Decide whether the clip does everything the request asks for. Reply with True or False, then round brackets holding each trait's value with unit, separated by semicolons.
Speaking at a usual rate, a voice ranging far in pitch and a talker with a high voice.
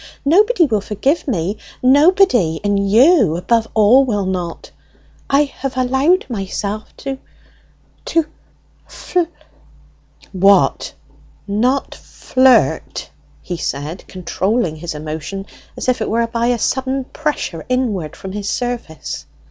False (115 wpm; 5.8 semitones; 225 Hz)